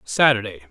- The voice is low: Yes, low, 110 Hz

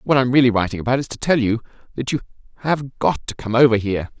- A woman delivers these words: No, male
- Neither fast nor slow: No, fast, 255 wpm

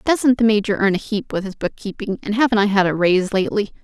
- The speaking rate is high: Yes, fast, 250 wpm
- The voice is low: No, high, 210 Hz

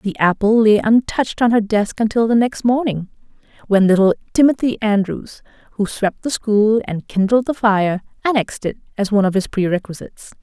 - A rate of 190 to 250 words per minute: No, average, 175 wpm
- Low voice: No, high, 215 Hz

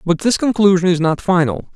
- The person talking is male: Yes, male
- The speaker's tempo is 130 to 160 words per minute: No, fast, 205 wpm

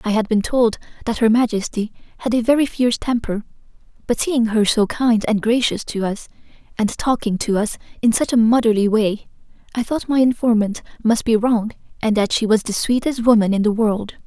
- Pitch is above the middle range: Yes, high, 225 Hz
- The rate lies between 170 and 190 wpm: No, average, 200 wpm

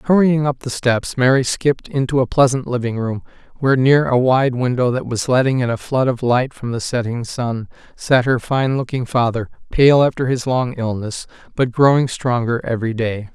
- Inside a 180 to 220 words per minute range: Yes, average, 195 wpm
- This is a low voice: Yes, low, 125 Hz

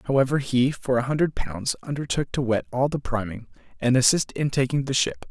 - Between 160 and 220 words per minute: Yes, fast, 205 wpm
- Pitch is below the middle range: Yes, low, 130 Hz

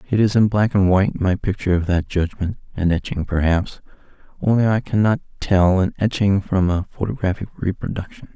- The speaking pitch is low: Yes, very low, 95 Hz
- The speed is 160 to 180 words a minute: Yes, average, 170 wpm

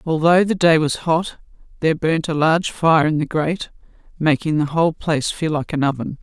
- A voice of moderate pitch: Yes, medium, 155 Hz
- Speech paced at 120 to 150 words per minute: No, fast, 205 wpm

